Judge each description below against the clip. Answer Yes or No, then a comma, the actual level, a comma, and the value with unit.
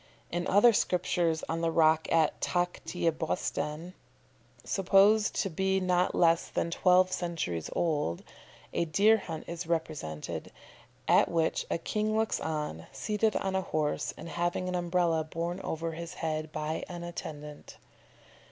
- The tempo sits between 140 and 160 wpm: Yes, average, 145 wpm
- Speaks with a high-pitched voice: No, medium, 170 Hz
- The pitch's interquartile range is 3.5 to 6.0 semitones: No, narrow, 2.5 semitones